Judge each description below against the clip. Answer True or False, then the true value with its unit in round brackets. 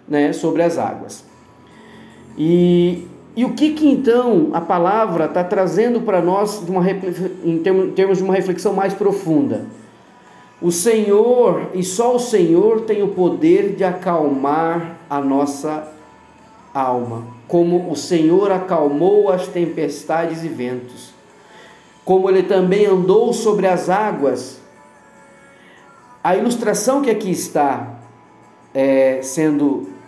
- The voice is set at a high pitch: False (180 Hz)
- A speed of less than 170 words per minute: True (125 wpm)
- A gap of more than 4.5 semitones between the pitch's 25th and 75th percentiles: True (5.0 semitones)